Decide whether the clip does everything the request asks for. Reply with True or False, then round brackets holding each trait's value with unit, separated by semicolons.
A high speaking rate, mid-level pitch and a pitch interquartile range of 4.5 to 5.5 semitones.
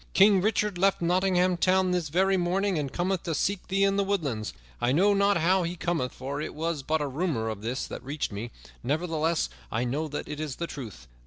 True (220 wpm; 170 Hz; 4.8 semitones)